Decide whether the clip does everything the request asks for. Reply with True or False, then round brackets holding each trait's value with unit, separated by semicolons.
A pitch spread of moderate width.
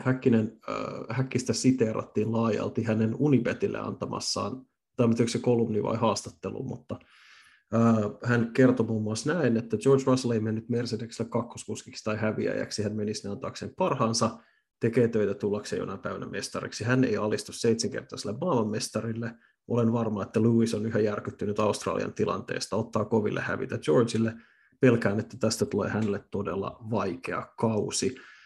False (1.9 semitones)